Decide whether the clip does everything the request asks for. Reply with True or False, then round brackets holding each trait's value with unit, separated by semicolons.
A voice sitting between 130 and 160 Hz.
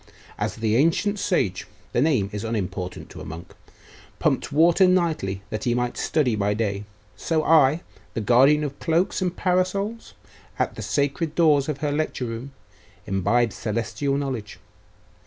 True (135 Hz)